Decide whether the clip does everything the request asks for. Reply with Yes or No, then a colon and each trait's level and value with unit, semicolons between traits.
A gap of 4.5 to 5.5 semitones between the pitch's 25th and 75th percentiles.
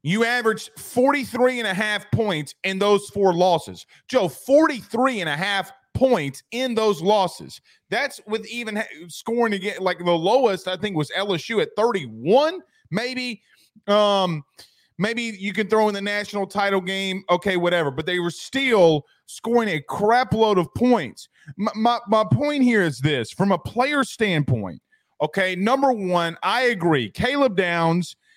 Yes: average, 4.9 semitones